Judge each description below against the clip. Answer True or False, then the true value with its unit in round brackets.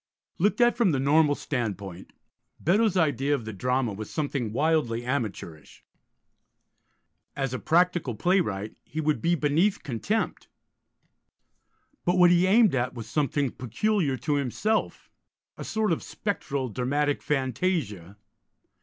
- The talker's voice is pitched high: False (145 Hz)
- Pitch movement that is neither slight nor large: False (6.4 semitones)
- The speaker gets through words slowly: True (130 wpm)